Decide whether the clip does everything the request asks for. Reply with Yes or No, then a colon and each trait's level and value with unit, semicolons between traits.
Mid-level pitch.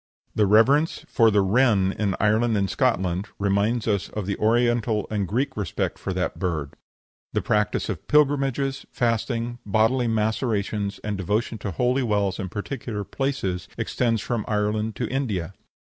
No: low, 110 Hz